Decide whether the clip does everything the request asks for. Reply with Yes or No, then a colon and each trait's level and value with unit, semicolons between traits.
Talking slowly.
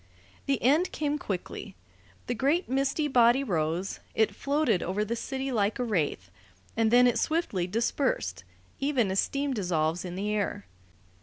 No: average, 155 wpm